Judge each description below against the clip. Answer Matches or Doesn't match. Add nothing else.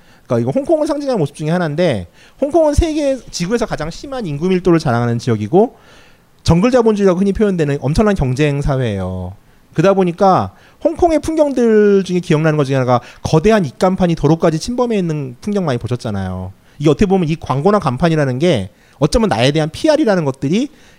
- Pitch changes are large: Matches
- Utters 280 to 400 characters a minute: Doesn't match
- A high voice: Doesn't match